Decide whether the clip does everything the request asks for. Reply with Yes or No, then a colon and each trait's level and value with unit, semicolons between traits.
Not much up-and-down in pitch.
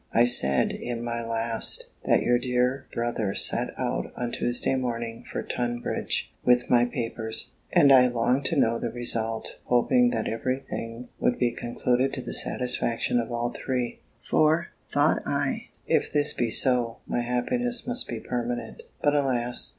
Yes: narrow, 1.7 semitones